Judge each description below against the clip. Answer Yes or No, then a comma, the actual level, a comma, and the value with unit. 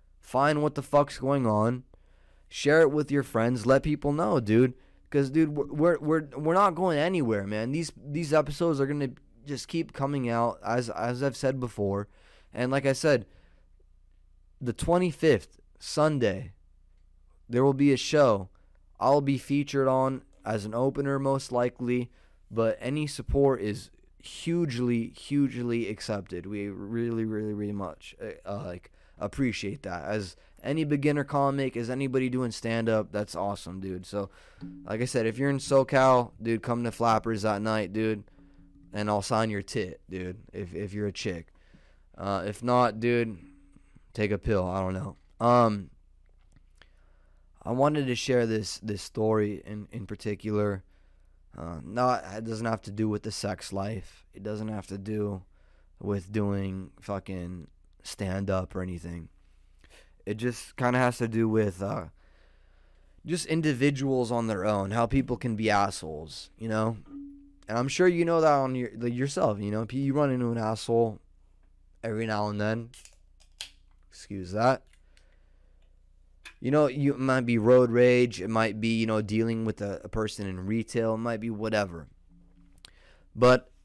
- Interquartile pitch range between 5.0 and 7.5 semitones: Yes, wide, 5.5 semitones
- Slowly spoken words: No, average, 165 wpm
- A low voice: Yes, low, 110 Hz